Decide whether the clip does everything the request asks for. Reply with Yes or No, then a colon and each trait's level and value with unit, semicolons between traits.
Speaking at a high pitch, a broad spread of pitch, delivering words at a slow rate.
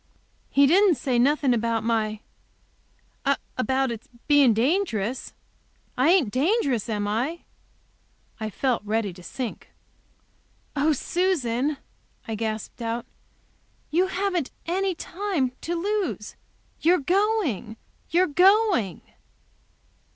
Yes: very high, 275 Hz; wide, 7.7 semitones; slow, 105 wpm